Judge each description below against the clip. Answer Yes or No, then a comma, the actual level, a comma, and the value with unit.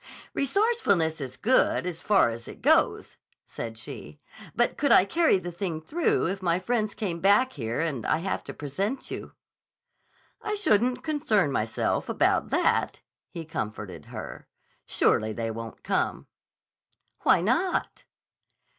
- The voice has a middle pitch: Yes, medium, 180 Hz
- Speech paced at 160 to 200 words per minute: No, average, 140 wpm